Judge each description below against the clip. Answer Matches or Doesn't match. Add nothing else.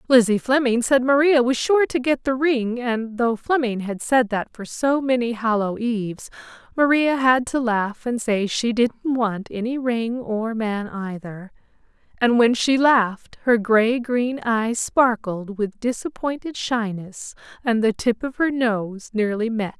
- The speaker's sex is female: Matches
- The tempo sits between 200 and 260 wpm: Doesn't match